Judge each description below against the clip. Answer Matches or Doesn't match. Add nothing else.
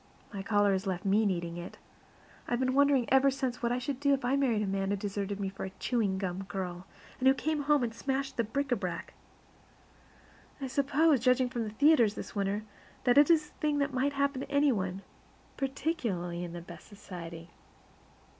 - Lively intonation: Matches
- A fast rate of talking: Matches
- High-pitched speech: Matches